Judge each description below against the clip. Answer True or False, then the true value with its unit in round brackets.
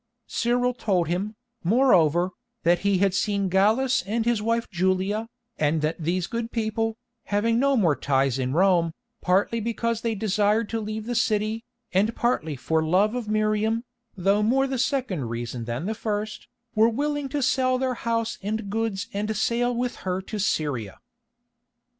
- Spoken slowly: False (165 wpm)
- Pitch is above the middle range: True (215 Hz)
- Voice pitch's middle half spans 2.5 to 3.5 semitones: False (4.1 semitones)